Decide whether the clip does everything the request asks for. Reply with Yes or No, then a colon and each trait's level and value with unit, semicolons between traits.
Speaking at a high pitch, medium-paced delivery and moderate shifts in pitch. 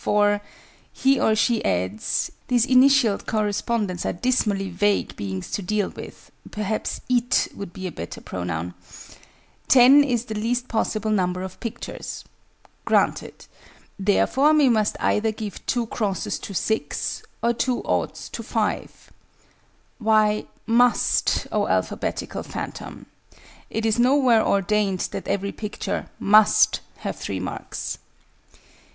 No: high, 215 Hz; slow, 125 wpm; average, 3.4 semitones